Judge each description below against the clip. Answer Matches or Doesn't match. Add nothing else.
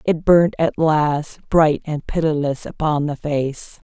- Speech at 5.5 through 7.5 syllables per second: Doesn't match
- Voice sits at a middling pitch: Matches